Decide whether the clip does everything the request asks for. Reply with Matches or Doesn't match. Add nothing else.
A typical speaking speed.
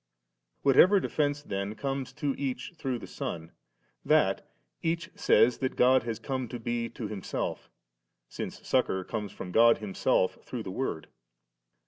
Matches